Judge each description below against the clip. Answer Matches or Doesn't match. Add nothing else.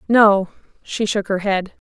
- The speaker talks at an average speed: Matches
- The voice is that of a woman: Matches